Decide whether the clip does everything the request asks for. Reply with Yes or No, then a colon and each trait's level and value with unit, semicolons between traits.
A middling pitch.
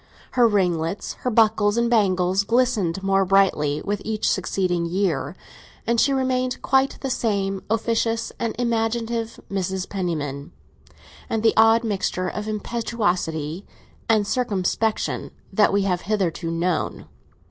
No: high, 205 Hz